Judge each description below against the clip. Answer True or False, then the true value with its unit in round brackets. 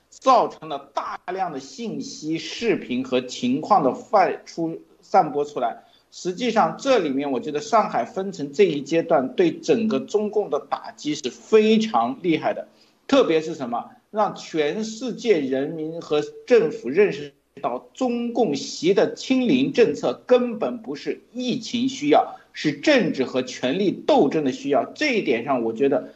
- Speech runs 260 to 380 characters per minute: False (235 characters per minute)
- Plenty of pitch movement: True (8.0 semitones)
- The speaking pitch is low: False (220 Hz)